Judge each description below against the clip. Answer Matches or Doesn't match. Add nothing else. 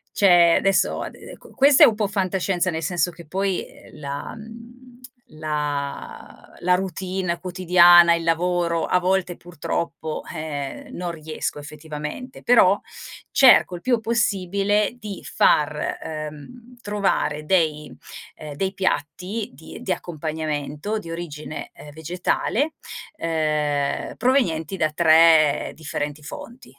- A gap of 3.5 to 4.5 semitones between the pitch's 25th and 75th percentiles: Matches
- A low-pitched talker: Doesn't match